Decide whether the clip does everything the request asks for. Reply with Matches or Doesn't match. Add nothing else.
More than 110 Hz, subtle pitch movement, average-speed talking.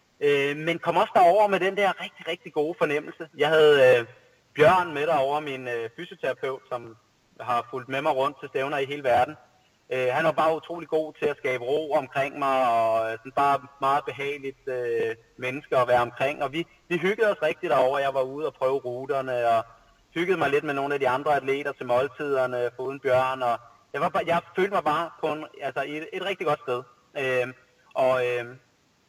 Doesn't match